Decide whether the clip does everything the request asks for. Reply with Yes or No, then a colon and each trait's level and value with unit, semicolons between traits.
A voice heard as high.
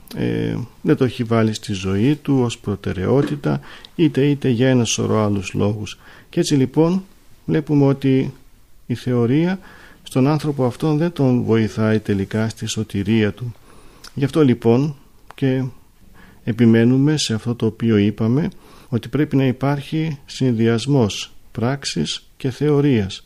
No: low, 125 Hz